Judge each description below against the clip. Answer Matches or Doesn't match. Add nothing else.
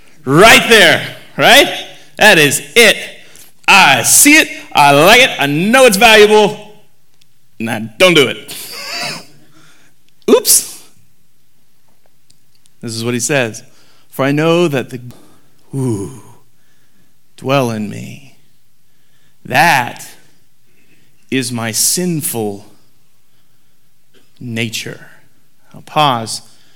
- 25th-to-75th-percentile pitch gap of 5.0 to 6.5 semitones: Matches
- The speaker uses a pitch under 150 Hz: Matches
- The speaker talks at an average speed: Doesn't match